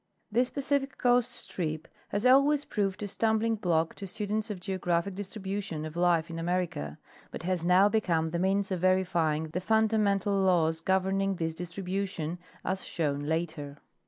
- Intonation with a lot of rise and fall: No, average, 3.7 semitones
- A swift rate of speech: No, average, 155 wpm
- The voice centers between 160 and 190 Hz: Yes, medium, 185 Hz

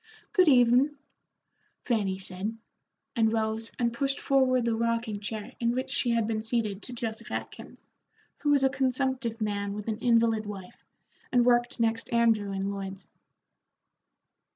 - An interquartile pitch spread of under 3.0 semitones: Yes, narrow, 2.5 semitones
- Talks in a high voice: Yes, high, 230 Hz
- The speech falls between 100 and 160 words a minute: Yes, average, 150 wpm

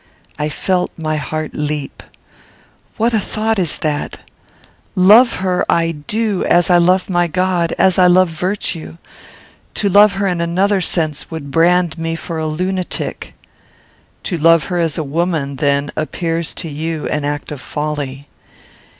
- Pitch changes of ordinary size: Yes, average, 3.2 semitones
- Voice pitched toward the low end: No, medium, 170 Hz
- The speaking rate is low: No, average, 155 wpm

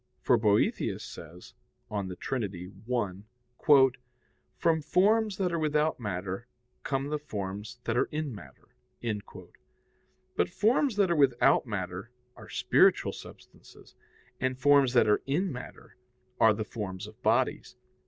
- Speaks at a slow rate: Yes, slow, 130 wpm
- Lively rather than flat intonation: Yes, wide, 6.8 semitones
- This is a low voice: Yes, low, 120 Hz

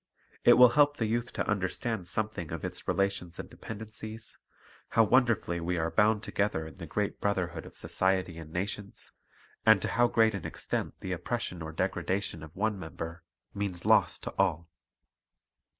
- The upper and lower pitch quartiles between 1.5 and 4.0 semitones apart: No, average, 4.4 semitones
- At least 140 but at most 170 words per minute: Yes, average, 165 wpm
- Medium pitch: No, low, 100 Hz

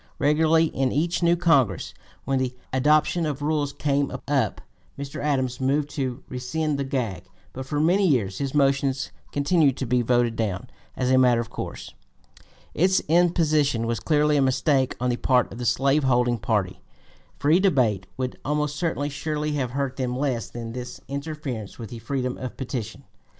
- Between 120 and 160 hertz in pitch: Yes, low, 135 Hz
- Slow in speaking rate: No, average, 175 wpm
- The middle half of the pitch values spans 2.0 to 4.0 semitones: Yes, average, 3.2 semitones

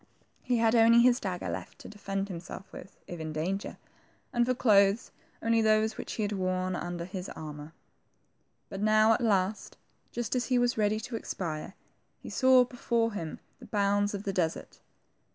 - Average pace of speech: Yes, average, 175 wpm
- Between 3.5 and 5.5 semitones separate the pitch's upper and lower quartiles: Yes, average, 3.8 semitones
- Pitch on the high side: Yes, high, 205 Hz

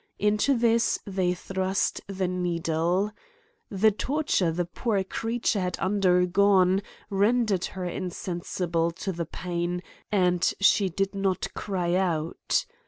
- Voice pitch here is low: No, medium, 185 Hz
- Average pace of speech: No, slow, 120 wpm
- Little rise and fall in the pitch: Yes, narrow, 2.2 semitones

